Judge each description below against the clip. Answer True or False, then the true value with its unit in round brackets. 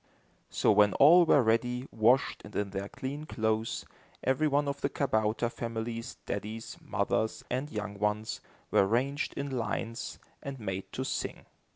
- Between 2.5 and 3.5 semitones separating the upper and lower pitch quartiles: False (4.1 semitones)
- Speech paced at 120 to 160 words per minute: True (155 wpm)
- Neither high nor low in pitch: False (115 Hz)